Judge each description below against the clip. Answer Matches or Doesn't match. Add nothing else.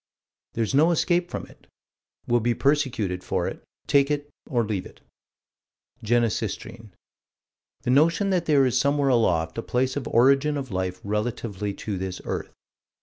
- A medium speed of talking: Matches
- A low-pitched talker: Matches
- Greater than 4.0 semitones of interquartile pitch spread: Matches